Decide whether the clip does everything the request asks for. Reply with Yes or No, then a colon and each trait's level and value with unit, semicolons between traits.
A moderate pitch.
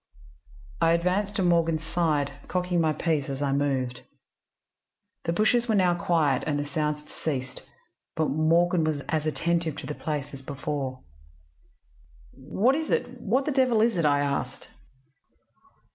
Yes: medium, 160 Hz